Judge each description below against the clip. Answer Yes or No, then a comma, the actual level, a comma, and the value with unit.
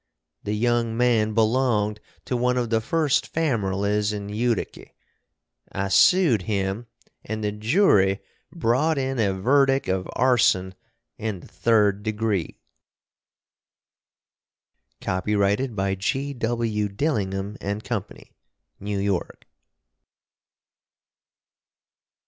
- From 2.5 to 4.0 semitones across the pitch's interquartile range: Yes, average, 3.6 semitones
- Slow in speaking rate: Yes, slow, 95 wpm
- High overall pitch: No, low, 110 Hz